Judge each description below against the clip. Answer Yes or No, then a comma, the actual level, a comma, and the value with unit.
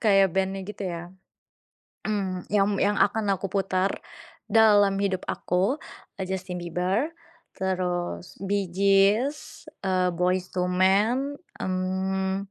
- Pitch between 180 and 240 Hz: Yes, high, 190 Hz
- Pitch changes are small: Yes, narrow, 1.6 semitones